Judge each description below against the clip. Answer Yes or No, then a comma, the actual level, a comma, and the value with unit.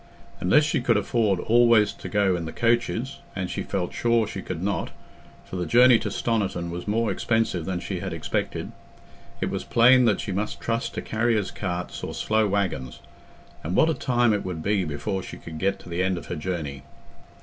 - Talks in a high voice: No, low, 100 Hz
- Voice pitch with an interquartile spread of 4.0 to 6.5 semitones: Yes, average, 4.5 semitones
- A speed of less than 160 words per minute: No, average, 195 wpm